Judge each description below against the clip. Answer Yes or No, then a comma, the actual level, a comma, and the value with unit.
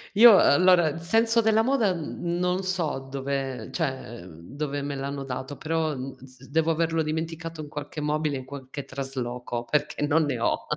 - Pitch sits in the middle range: Yes, medium, 150 Hz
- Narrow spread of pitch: No, average, 3.6 semitones